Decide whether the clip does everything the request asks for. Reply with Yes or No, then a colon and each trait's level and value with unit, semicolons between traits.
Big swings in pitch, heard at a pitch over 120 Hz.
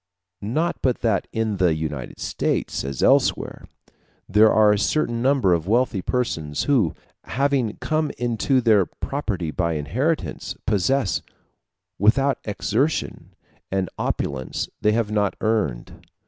No: wide, 5.7 semitones; low, 110 Hz